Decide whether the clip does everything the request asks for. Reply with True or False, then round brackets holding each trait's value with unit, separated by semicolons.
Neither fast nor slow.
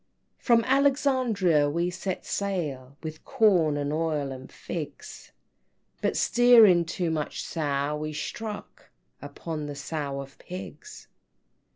False (125 wpm)